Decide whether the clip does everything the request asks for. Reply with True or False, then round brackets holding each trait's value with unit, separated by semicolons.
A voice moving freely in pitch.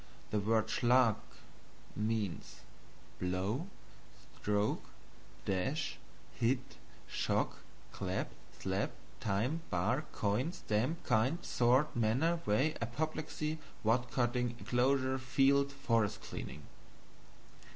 False (4.3 semitones)